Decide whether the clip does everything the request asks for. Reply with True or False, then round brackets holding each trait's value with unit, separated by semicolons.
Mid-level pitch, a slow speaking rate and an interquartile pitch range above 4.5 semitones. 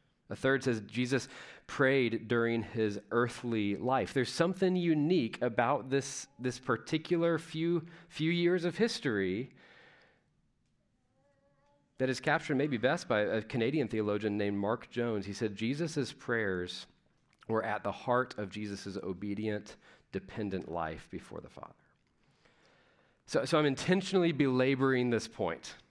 False (125 Hz; 130 wpm; 5.2 semitones)